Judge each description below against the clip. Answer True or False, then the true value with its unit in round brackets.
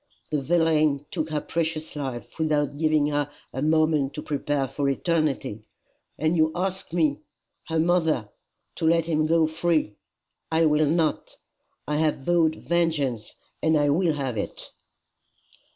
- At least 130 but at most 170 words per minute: True (145 wpm)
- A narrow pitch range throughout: True (2.0 semitones)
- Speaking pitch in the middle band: True (155 Hz)